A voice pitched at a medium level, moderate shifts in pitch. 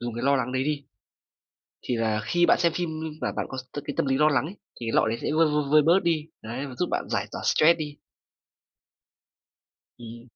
Yes: medium, 145 Hz; average, 4.4 semitones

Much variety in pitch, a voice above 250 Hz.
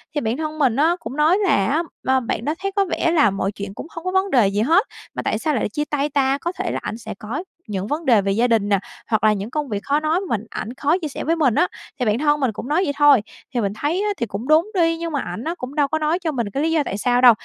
Yes: wide, 6.2 semitones; very high, 285 Hz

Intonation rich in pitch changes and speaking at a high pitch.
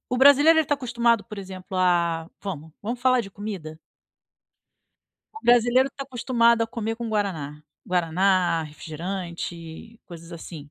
Yes: wide, 5.9 semitones; high, 195 Hz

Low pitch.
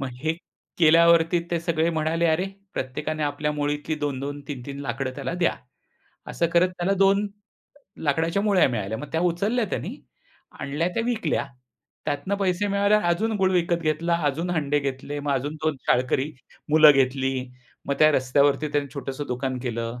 No: medium, 155 Hz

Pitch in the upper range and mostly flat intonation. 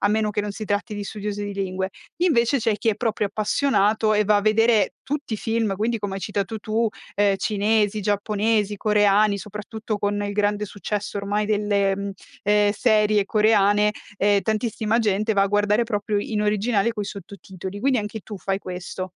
Yes: high, 210 Hz; narrow, 1.3 semitones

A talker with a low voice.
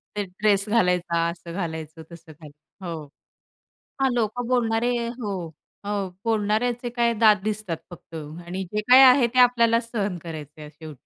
No: high, 200 Hz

